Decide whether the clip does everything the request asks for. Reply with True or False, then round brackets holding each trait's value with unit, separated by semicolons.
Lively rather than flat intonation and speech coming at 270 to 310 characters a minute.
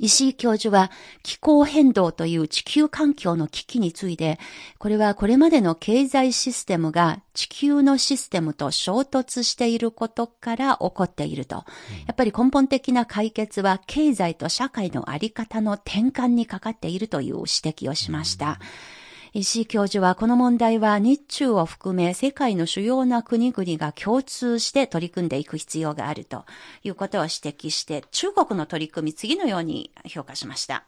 False (6.8 semitones; 330 characters per minute)